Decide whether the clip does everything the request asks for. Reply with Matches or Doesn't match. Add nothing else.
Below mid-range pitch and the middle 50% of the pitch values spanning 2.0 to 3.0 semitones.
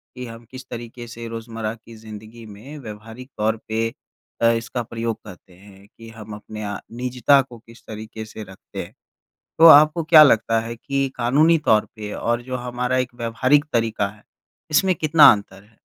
Matches